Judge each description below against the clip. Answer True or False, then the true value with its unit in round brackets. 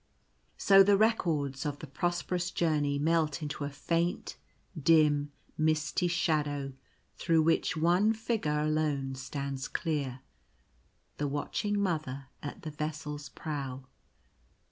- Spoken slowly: True (120 wpm)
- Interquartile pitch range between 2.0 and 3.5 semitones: True (2.9 semitones)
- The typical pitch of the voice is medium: True (155 Hz)